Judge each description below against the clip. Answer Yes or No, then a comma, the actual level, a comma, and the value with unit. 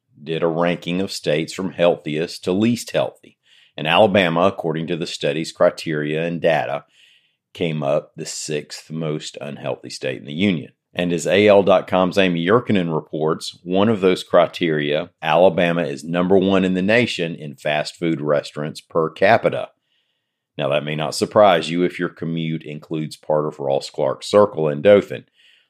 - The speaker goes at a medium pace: Yes, average, 160 wpm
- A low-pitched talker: Yes, very low, 85 Hz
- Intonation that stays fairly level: No, average, 3.2 semitones